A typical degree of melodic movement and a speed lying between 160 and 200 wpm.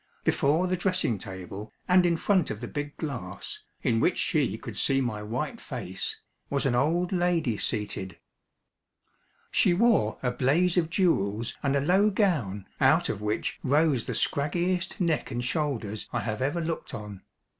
No: wide, 8.0 semitones; average, 165 wpm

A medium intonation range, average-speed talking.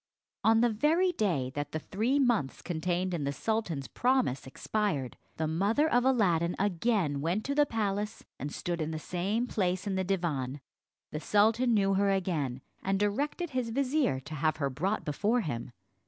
No: wide, 6.3 semitones; average, 175 wpm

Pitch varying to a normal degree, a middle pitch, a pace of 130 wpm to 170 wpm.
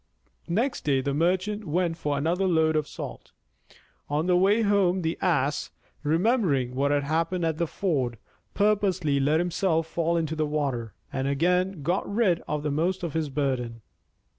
Yes: average, 4.0 semitones; medium, 165 Hz; average, 165 wpm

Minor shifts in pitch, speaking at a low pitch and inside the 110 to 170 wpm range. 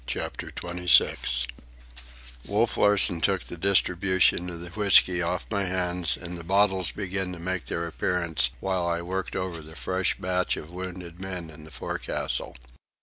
Yes: narrow, 1.8 semitones; very low, 90 Hz; average, 155 wpm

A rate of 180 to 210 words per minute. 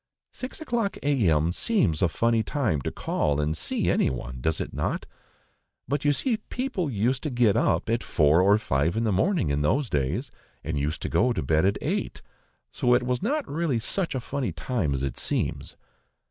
Yes: average, 200 wpm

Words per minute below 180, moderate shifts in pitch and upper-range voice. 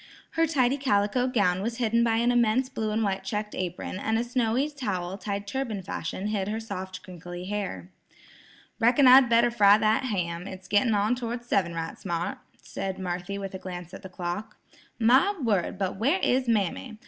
No: average, 185 wpm; average, 4.2 semitones; high, 210 Hz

